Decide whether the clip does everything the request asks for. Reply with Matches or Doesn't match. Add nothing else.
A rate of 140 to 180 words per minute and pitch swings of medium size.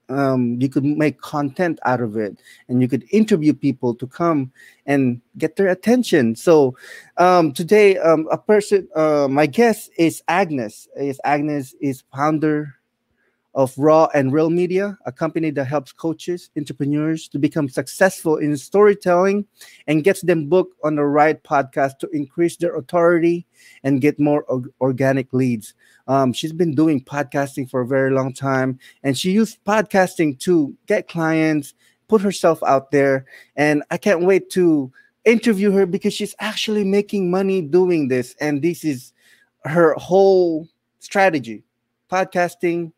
Matches